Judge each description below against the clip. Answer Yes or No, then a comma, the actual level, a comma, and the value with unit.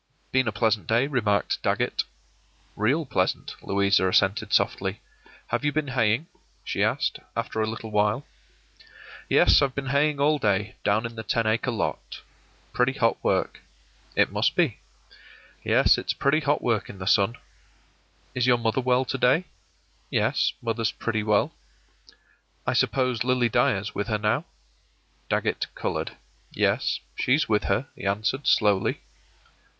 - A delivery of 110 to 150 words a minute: Yes, average, 145 wpm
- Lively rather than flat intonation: No, average, 3.8 semitones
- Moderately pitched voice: No, low, 115 Hz